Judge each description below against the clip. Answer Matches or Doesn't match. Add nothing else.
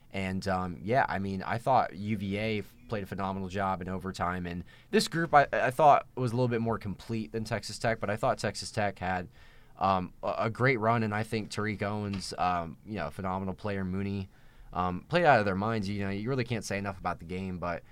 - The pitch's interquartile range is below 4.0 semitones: Matches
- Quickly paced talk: Matches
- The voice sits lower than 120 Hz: Matches